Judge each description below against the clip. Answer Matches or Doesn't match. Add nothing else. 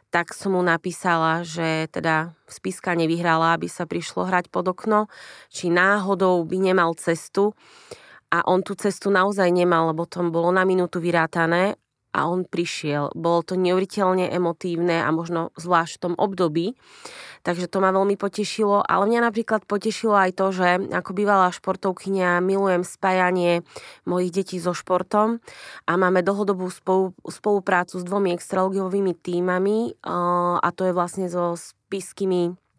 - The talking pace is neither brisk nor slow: Matches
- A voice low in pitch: Doesn't match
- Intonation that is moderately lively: Doesn't match